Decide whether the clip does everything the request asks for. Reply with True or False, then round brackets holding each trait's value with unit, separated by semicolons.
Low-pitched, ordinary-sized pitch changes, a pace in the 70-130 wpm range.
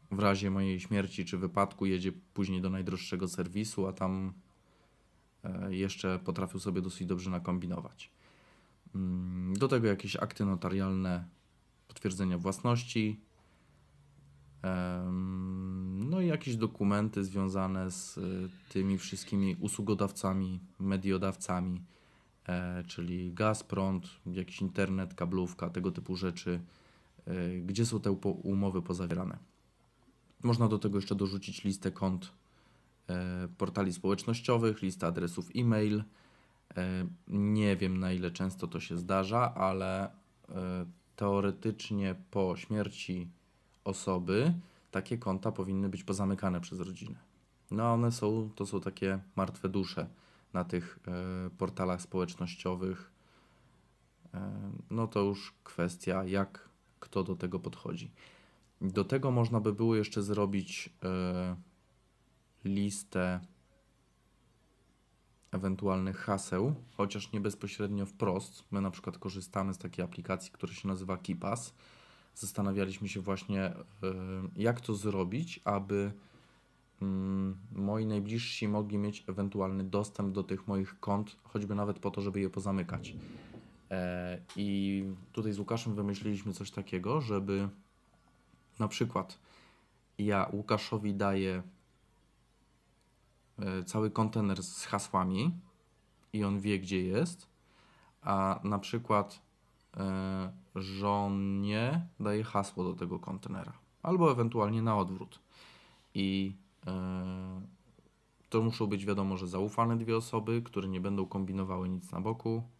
False (95 Hz; 1.9 semitones; 115 wpm)